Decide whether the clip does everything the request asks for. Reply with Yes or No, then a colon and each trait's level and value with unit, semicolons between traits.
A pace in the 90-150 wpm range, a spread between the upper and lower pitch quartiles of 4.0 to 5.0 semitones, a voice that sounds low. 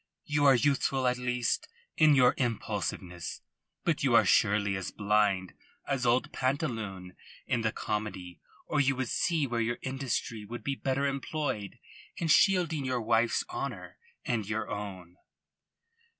Yes: average, 145 wpm; average, 4.7 semitones; low, 120 Hz